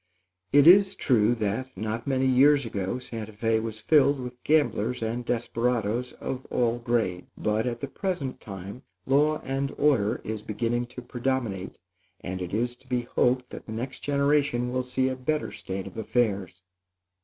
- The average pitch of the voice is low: Yes, low, 120 Hz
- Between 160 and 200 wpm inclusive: Yes, average, 165 wpm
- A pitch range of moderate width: Yes, average, 3.1 semitones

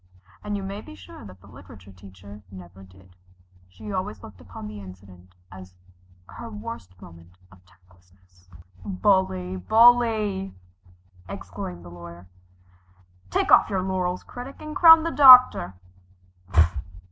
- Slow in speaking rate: Yes, slow, 130 wpm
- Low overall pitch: Yes, very low, 95 Hz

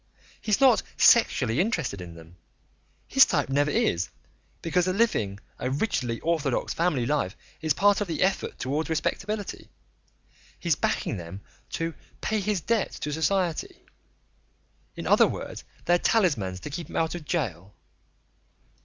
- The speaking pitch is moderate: Yes, medium, 160 Hz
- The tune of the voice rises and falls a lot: Yes, wide, 7.7 semitones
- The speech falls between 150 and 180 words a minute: No, average, 140 wpm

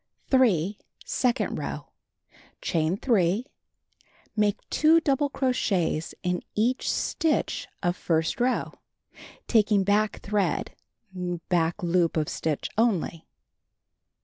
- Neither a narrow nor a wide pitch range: No, wide, 6.1 semitones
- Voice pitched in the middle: No, high, 200 Hz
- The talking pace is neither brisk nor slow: No, slow, 100 wpm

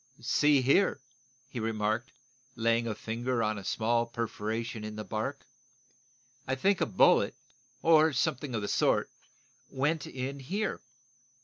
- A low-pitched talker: Yes, low, 120 Hz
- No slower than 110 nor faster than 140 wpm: Yes, slow, 135 wpm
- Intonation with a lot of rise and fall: No, average, 4.0 semitones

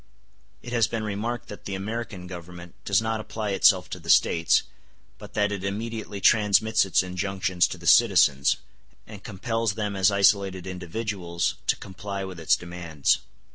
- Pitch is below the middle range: Yes, low, 100 Hz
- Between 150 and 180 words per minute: Yes, average, 160 wpm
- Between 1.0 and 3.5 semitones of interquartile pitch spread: Yes, average, 3.1 semitones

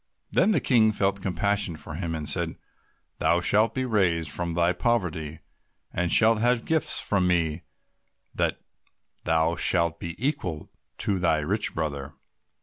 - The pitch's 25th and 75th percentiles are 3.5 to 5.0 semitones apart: Yes, average, 4.6 semitones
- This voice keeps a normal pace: Yes, average, 150 wpm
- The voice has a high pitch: No, very low, 90 Hz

